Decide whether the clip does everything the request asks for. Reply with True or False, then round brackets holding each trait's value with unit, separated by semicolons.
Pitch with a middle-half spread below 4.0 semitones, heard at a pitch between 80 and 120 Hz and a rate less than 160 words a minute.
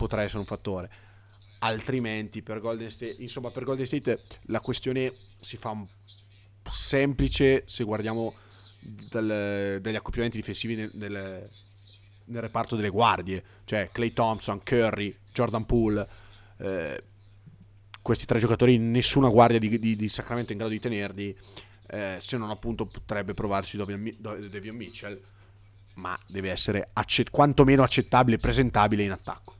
True (2.7 semitones; 105 Hz; 135 wpm)